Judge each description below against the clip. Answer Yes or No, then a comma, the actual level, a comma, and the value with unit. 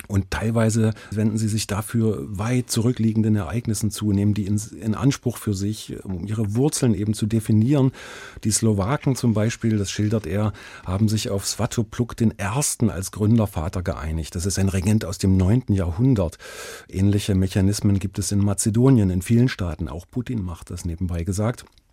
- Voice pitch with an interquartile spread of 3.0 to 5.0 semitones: No, narrow, 2.4 semitones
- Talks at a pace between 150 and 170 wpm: Yes, average, 165 wpm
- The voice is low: Yes, low, 105 Hz